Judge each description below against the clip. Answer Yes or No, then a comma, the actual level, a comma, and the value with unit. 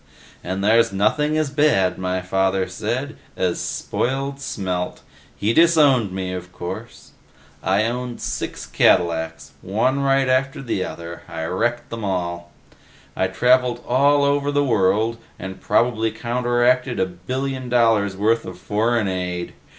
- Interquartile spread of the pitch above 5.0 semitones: Yes, wide, 5.6 semitones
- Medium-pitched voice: No, low, 115 Hz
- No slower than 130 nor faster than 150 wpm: Yes, slow, 135 wpm